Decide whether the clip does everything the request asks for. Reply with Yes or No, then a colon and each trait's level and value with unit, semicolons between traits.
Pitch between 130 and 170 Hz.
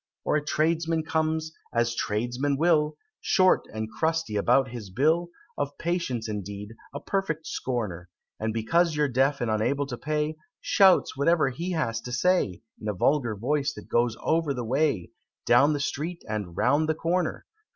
Yes: medium, 140 Hz